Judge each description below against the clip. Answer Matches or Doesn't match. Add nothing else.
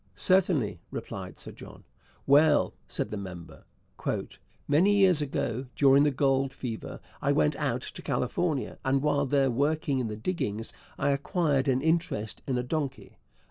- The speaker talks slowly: Doesn't match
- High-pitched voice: Doesn't match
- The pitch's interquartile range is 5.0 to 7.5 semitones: Doesn't match